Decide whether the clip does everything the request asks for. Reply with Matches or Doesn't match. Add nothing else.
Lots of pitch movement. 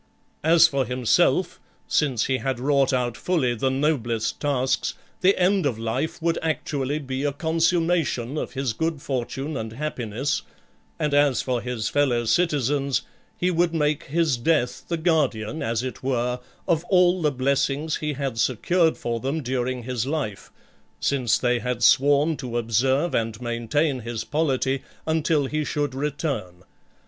Doesn't match